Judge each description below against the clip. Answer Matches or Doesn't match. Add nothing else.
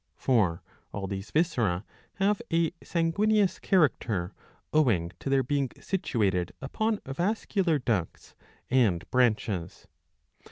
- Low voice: Matches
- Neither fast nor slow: Doesn't match